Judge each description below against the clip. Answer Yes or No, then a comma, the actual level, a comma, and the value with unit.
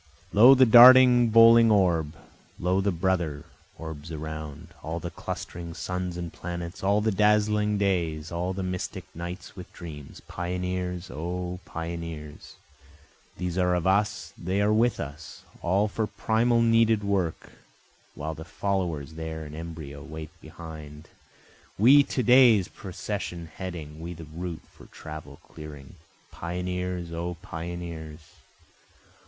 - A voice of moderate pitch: No, very low, 90 Hz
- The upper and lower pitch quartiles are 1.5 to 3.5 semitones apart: No, average, 3.9 semitones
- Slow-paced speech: Yes, slow, 130 wpm